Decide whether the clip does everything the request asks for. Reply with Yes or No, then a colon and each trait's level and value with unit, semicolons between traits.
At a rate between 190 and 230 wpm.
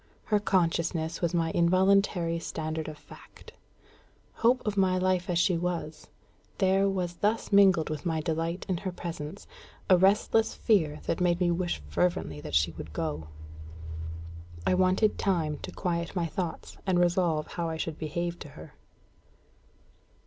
No: average, 155 wpm